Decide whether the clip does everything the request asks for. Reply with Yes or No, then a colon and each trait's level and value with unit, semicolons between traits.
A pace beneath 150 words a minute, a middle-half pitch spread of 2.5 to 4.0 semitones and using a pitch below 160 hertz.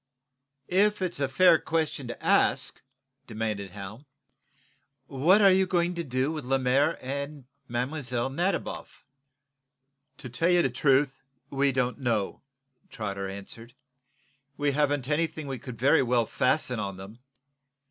No: slow, 135 wpm; average, 4.7 semitones; low, 135 Hz